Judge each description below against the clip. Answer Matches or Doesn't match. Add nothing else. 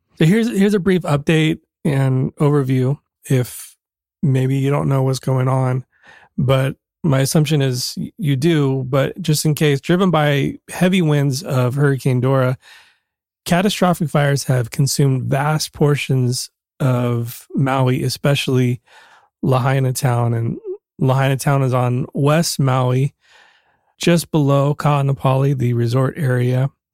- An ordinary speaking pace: Doesn't match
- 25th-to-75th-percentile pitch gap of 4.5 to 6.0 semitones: Doesn't match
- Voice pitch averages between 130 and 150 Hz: Matches